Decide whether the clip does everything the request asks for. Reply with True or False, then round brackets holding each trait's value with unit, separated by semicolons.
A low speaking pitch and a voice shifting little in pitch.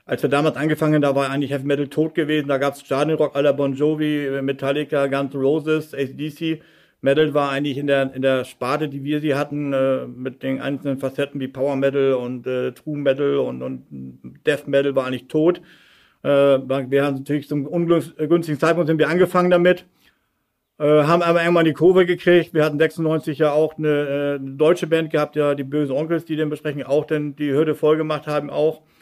False (145 Hz; 2.1 semitones)